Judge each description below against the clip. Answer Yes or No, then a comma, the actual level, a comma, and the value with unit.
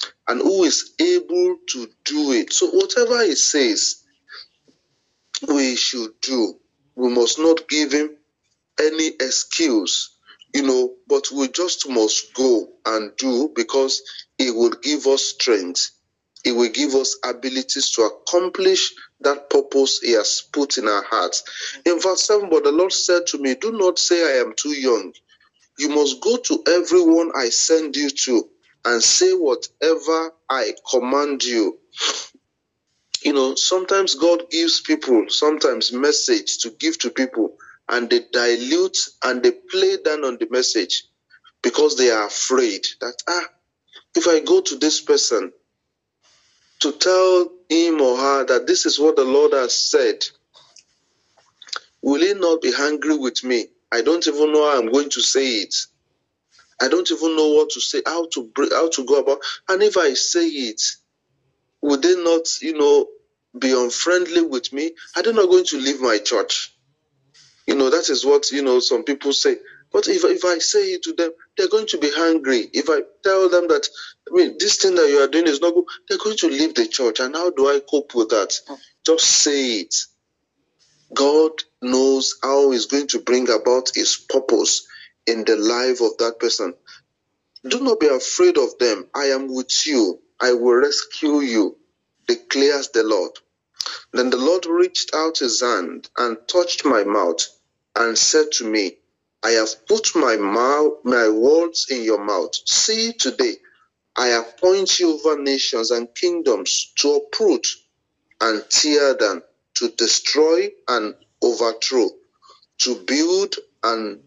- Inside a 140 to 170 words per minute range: Yes, average, 165 wpm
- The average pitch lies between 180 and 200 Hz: Yes, medium, 185 Hz